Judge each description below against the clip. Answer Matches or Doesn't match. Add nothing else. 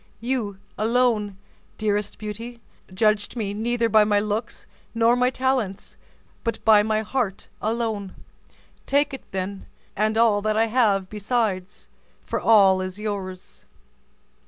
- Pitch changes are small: Matches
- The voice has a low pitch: Doesn't match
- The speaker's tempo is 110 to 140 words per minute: Matches